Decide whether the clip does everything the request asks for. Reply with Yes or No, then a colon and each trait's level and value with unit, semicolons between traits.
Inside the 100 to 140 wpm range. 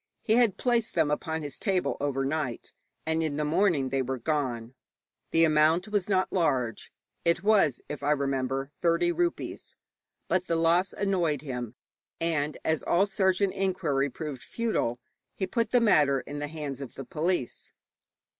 No: average, 165 wpm